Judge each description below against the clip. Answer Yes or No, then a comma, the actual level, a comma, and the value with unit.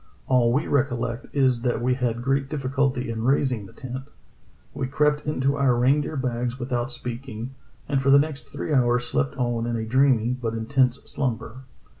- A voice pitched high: No, low, 130 Hz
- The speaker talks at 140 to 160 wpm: No, average, 180 wpm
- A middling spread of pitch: No, narrow, 2.3 semitones